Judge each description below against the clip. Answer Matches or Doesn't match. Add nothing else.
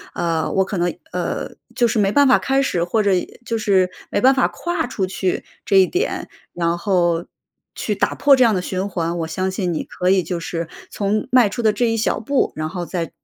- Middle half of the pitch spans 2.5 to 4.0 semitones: Doesn't match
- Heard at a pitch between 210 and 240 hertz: Doesn't match